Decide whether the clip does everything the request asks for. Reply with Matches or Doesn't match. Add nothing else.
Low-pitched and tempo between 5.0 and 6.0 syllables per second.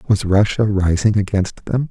Doesn't match